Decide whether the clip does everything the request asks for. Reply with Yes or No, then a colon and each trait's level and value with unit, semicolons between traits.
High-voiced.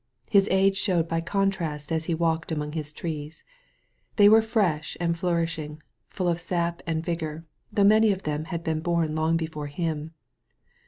No: medium, 165 Hz